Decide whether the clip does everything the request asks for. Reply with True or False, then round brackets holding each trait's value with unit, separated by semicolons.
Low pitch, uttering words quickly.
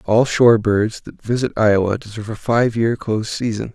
False (110 Hz; 190 wpm)